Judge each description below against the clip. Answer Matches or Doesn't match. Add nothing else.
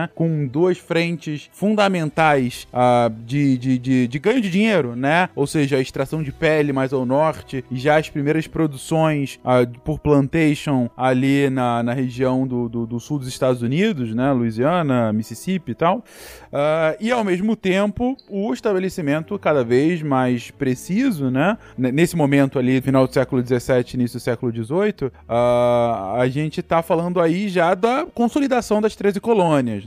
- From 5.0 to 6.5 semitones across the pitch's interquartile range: Matches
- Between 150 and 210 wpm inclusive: Matches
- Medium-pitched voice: Matches